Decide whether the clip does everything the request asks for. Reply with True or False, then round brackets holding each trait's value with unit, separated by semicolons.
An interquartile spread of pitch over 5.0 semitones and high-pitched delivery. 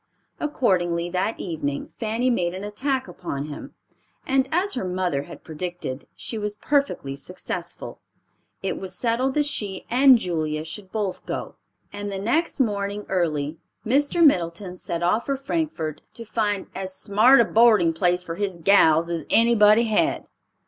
True (5.5 semitones; 200 Hz)